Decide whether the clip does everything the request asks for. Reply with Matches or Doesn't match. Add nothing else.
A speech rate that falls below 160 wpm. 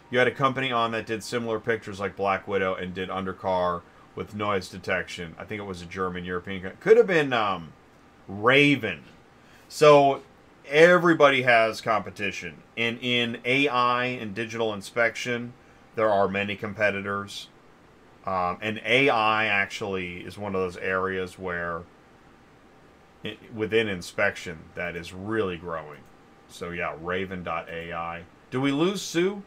Matches